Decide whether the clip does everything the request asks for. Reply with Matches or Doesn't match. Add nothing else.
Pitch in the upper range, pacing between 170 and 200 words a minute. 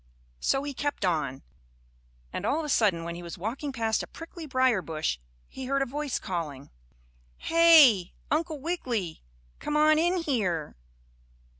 Doesn't match